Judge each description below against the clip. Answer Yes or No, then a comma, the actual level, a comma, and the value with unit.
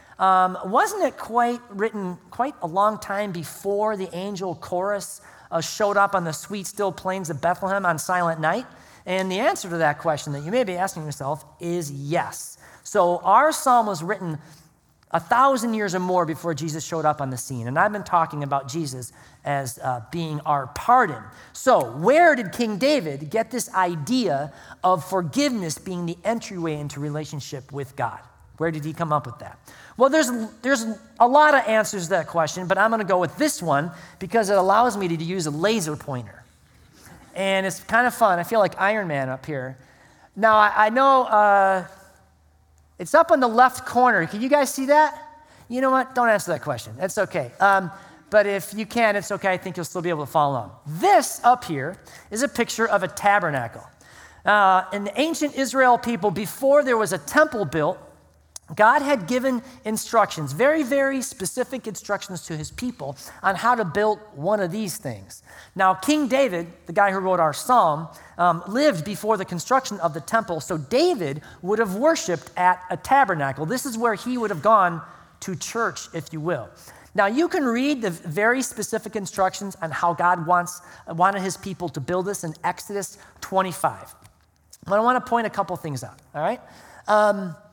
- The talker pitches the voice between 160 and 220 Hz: Yes, high, 190 Hz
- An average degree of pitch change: No, wide, 5.7 semitones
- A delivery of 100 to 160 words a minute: No, average, 195 wpm